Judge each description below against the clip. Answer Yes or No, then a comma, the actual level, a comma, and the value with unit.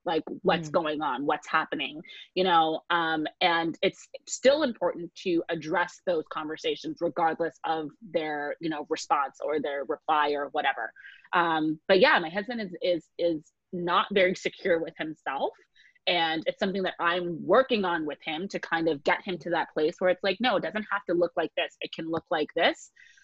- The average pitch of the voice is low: No, medium, 170 Hz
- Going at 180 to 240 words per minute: Yes, average, 190 wpm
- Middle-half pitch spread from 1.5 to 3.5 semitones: Yes, average, 2.9 semitones